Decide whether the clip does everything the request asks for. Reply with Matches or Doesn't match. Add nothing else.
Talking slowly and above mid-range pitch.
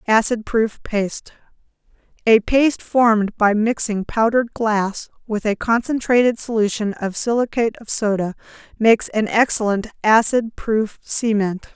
Matches